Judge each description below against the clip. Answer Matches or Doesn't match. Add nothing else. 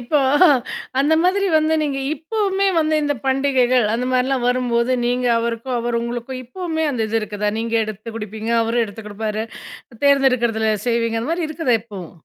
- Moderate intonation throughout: Matches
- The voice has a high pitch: Matches